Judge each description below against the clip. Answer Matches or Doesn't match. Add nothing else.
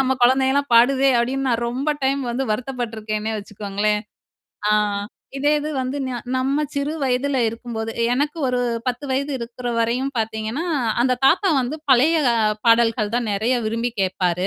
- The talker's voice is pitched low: Doesn't match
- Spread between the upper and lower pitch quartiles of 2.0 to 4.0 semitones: Matches